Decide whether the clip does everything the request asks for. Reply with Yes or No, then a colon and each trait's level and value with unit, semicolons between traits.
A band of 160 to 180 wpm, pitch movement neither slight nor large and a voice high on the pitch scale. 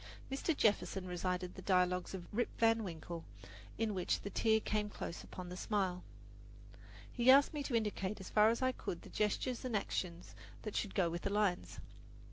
No: average, 190 wpm; average, 3.8 semitones; high, 200 Hz